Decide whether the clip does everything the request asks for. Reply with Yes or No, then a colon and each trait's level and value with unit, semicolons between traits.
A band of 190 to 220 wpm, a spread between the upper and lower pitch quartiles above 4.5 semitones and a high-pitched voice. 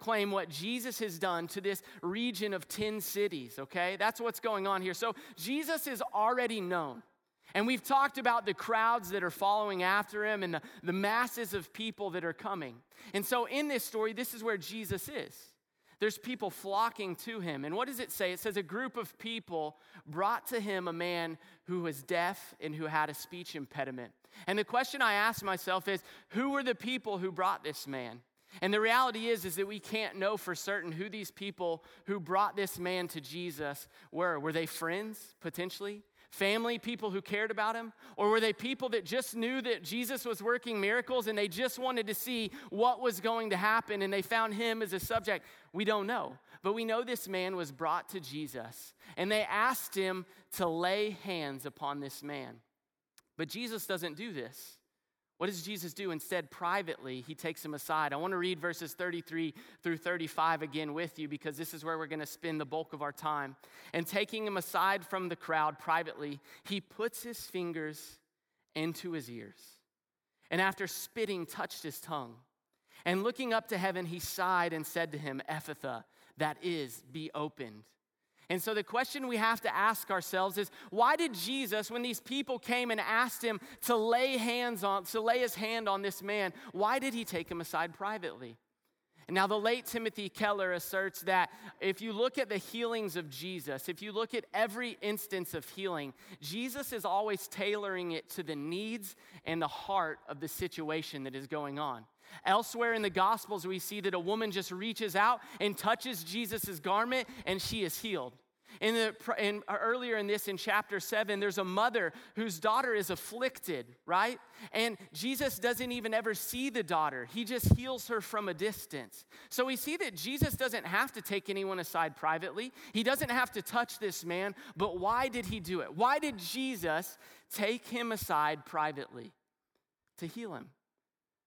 Yes: average, 195 wpm; average, 5.0 semitones; high, 200 Hz